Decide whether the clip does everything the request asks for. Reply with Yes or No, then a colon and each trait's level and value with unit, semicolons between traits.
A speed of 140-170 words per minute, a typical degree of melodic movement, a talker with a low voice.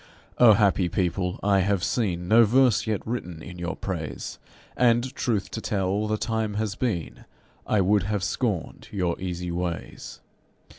Yes: average, 155 wpm; average, 3.6 semitones; low, 100 Hz